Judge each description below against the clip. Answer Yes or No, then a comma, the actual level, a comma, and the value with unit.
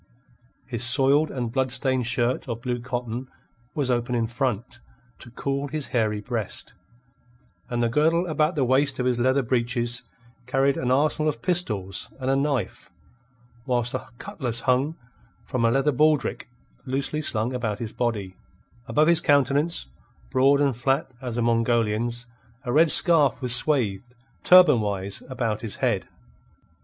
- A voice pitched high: No, low, 125 Hz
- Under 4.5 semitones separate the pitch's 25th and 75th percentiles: Yes, average, 3.0 semitones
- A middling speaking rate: Yes, average, 150 wpm